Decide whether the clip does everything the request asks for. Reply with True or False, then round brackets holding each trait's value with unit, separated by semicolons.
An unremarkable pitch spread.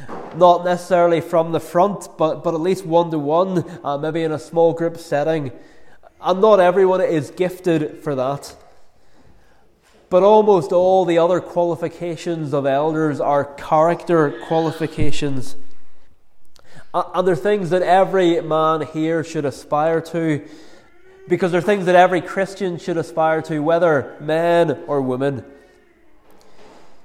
False (2.3 semitones)